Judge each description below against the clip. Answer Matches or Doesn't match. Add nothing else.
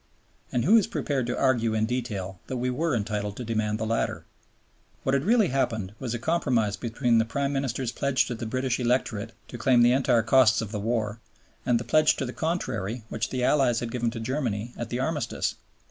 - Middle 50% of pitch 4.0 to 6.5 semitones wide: Doesn't match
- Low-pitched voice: Matches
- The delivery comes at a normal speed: Doesn't match